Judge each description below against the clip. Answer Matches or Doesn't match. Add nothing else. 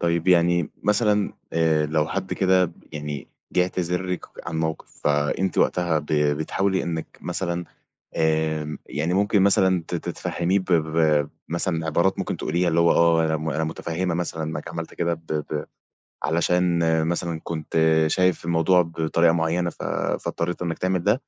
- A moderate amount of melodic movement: Doesn't match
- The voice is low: Matches